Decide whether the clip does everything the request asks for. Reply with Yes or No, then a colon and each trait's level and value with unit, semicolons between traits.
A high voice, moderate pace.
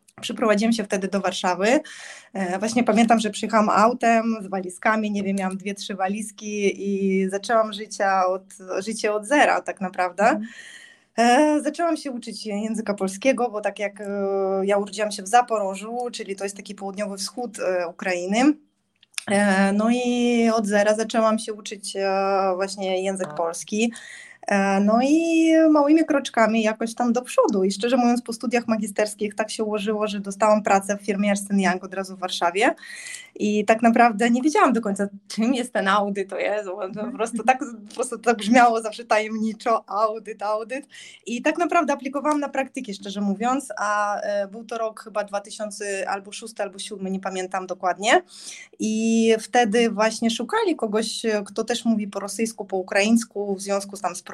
No: high, 215 Hz; fast, 165 wpm